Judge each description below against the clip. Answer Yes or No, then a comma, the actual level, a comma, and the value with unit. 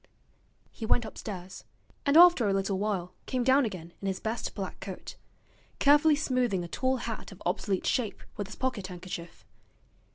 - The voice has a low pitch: No, high, 210 Hz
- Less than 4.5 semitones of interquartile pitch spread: No, average, 5.3 semitones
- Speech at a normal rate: Yes, average, 165 wpm